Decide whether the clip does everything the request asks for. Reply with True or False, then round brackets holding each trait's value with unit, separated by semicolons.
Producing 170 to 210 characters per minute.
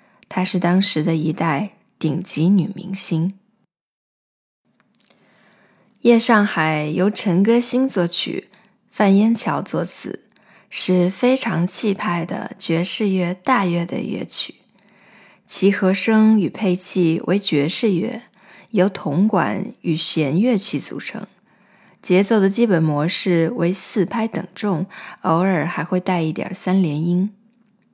True (175 characters per minute)